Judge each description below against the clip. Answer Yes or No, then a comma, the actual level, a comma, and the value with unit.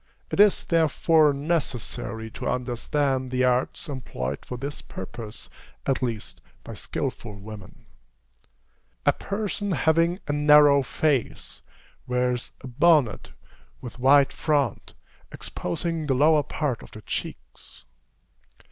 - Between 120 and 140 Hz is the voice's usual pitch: Yes, low, 135 Hz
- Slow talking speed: Yes, slow, 115 wpm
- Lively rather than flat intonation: No, average, 3.9 semitones